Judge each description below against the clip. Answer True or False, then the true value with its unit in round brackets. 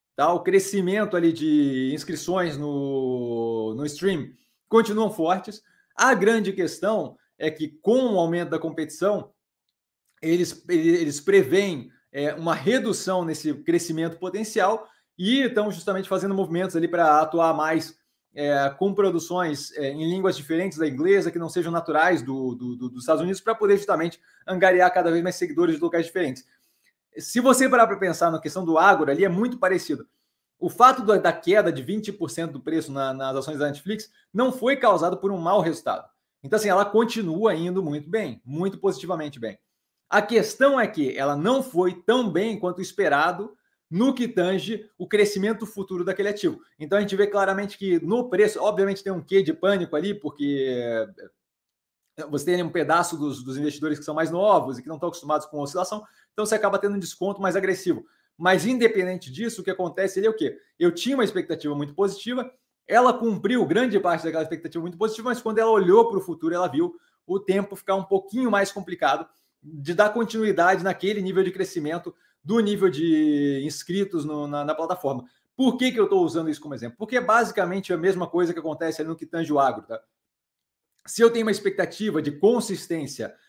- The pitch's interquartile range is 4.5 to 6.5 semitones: True (4.8 semitones)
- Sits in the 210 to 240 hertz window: False (185 Hz)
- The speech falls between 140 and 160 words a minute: False (185 wpm)